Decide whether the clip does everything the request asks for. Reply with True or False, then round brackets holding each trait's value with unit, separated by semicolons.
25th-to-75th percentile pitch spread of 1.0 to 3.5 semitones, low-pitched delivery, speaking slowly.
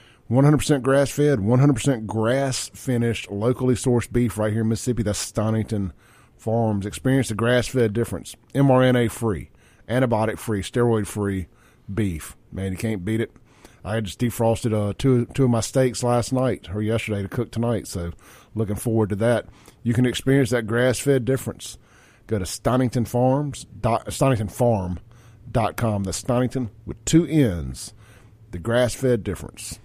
True (2.8 semitones; 115 Hz; 130 wpm)